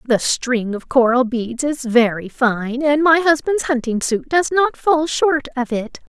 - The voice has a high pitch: Yes, very high, 265 Hz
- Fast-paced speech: No, average, 185 wpm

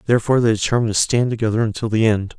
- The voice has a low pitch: Yes, low, 110 Hz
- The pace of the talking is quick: Yes, fast, 225 wpm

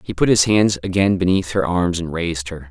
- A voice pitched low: Yes, very low, 90 Hz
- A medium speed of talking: No, fast, 245 wpm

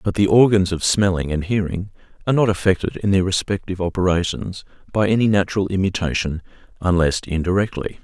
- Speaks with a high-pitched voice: No, very low, 95 Hz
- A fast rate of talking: No, average, 150 wpm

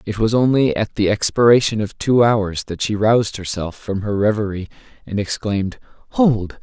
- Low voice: Yes, low, 105 Hz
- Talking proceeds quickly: No, average, 170 wpm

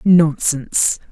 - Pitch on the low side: No, medium, 160 Hz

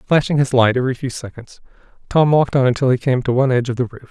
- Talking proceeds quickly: Yes, fast, 265 wpm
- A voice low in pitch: Yes, low, 130 Hz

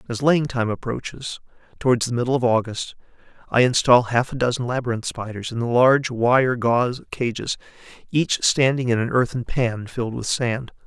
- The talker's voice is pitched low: Yes, low, 120 Hz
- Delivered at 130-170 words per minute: Yes, average, 165 wpm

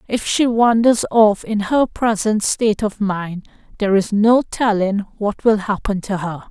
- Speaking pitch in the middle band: No, high, 210 Hz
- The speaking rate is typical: Yes, average, 175 wpm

